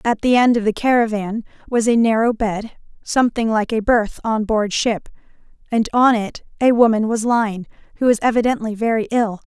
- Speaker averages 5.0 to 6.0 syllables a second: Yes, 5.2 syllables/s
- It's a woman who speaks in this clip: Yes, female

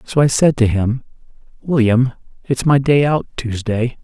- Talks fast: No, average, 165 wpm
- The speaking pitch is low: Yes, low, 125 Hz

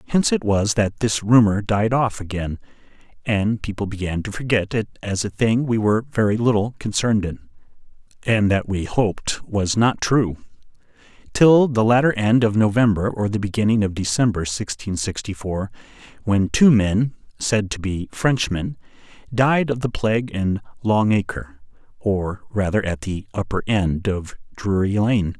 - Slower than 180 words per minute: Yes, average, 160 wpm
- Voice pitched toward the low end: Yes, low, 105 Hz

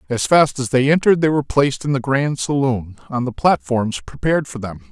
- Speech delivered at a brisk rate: Yes, fast, 220 wpm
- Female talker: No, male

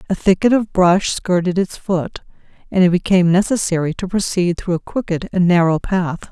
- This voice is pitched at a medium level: Yes, medium, 180 Hz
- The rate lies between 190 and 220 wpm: No, average, 180 wpm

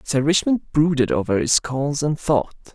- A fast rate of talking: No, average, 175 wpm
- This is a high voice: No, medium, 140 Hz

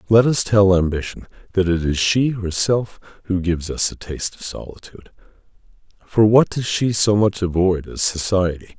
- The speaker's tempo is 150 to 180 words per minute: Yes, average, 170 wpm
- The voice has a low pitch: Yes, very low, 95 Hz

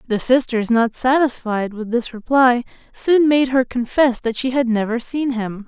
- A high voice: Yes, high, 245 Hz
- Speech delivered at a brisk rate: No, average, 180 wpm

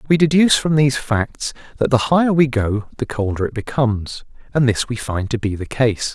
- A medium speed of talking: No, fast, 215 wpm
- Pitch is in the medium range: No, low, 125 Hz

